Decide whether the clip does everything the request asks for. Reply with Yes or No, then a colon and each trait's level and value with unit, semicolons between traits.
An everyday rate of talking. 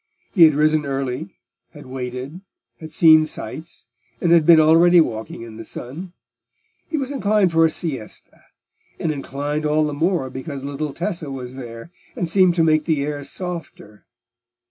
Yes: average, 165 wpm